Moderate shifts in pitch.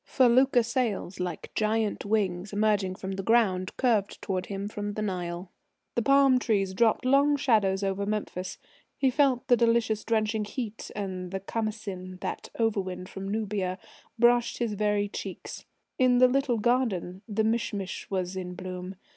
Yes: average, 3.8 semitones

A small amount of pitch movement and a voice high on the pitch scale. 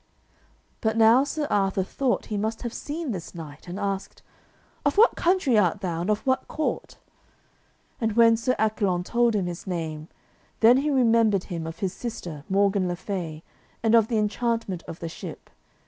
No: average, 4.7 semitones; high, 210 Hz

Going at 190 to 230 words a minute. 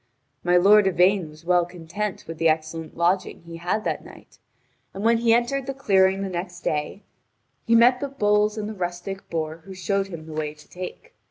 Yes: average, 200 wpm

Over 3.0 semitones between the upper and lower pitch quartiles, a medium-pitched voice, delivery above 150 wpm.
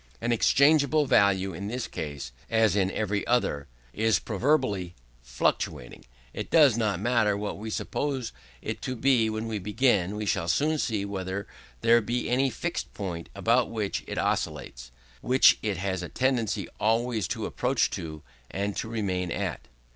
No: average, 4.1 semitones; low, 110 Hz; average, 160 wpm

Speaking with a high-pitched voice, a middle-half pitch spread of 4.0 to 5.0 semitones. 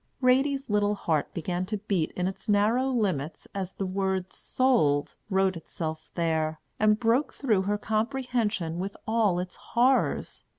Yes: high, 200 Hz; average, 4.4 semitones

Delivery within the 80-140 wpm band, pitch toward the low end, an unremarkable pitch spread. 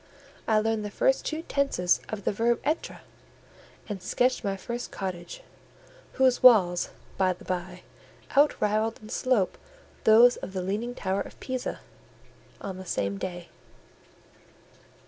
No: slow, 135 wpm; high, 215 Hz; average, 4.7 semitones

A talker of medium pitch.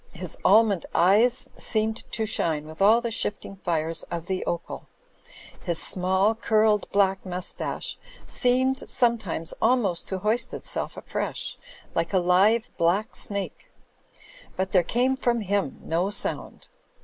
No: high, 200 Hz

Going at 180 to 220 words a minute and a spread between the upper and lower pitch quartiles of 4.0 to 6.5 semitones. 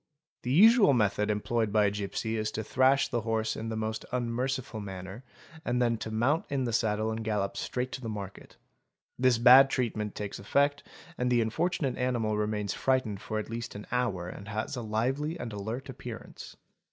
No: average, 190 wpm; average, 3.2 semitones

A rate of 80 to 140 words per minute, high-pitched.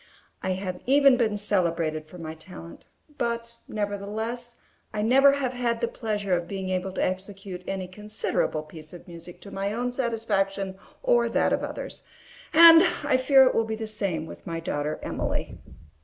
No: average, 170 wpm; high, 205 Hz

